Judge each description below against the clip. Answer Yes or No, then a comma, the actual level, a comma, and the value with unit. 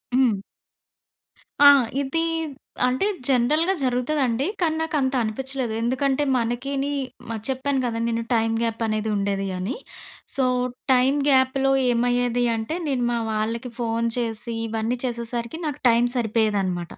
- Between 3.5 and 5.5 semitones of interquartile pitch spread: No, average, 2.9 semitones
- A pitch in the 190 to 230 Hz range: No, high, 245 Hz